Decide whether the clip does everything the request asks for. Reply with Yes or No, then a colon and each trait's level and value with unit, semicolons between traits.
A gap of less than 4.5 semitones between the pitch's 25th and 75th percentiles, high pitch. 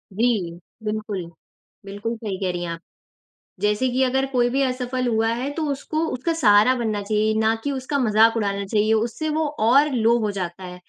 Yes: average, 3.7 semitones; high, 225 Hz